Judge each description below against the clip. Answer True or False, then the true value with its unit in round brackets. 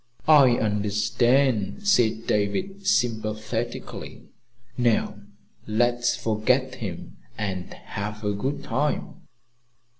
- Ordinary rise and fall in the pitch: True (3.2 semitones)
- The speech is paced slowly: True (85 wpm)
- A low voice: True (115 Hz)